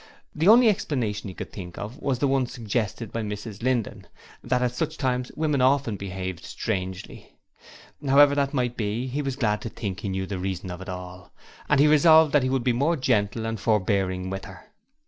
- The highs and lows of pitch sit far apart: Yes, wide, 5.8 semitones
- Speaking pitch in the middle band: No, low, 115 Hz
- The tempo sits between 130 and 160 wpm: No, fast, 205 wpm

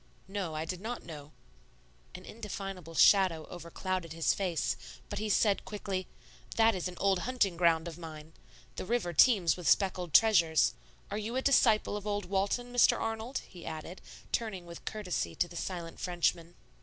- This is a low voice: No, medium, 185 Hz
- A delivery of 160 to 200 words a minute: Yes, average, 170 wpm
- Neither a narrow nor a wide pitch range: Yes, average, 3.8 semitones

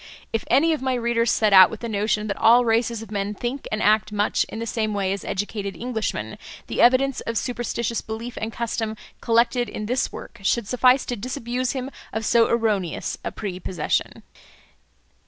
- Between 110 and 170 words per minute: No, average, 185 wpm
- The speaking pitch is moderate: No, high, 230 Hz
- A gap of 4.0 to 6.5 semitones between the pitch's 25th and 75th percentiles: No, narrow, 2.4 semitones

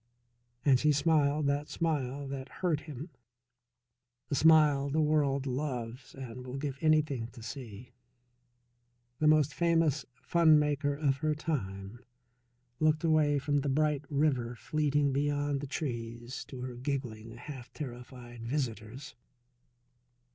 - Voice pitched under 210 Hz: Yes, medium, 140 Hz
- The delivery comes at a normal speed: No, slow, 125 wpm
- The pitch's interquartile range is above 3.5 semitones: No, average, 3.2 semitones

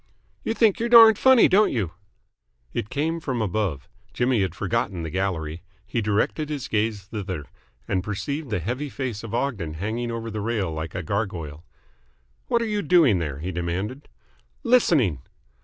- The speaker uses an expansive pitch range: Yes, wide, 7.5 semitones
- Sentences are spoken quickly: No, average, 165 wpm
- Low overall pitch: Yes, low, 110 Hz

